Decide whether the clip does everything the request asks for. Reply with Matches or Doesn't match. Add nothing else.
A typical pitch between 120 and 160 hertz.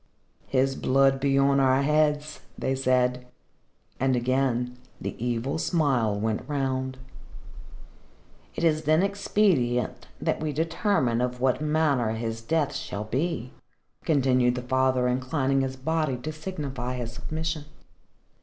Matches